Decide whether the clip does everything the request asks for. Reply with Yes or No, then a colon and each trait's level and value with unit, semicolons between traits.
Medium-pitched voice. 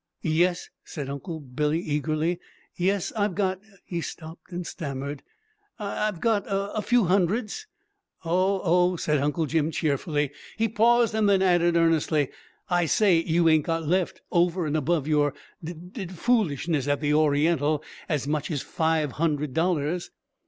Yes: medium, 165 Hz